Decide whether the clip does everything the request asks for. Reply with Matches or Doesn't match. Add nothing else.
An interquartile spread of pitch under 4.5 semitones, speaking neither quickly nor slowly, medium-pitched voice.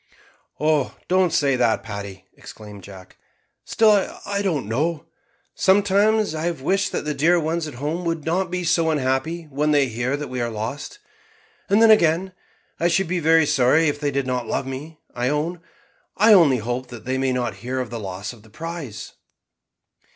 Doesn't match